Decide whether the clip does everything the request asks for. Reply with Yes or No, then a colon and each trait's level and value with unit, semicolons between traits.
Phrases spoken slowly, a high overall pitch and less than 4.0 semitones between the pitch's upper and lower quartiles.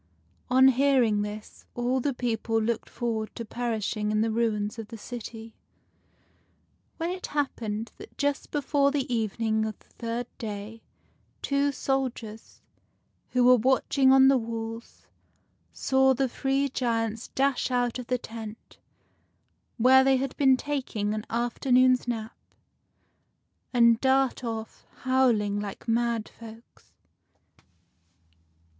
Yes: slow, 125 wpm; high, 240 Hz; average, 2.9 semitones